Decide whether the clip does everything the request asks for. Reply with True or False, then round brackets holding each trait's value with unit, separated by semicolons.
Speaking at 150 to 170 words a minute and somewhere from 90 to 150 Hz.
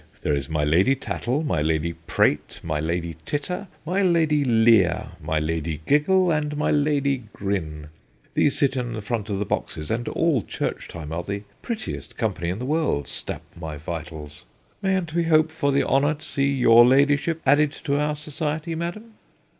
False (180 wpm; 135 Hz)